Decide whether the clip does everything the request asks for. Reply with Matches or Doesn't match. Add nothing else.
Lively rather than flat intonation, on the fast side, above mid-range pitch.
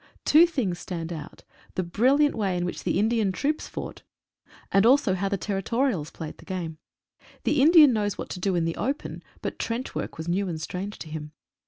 Matches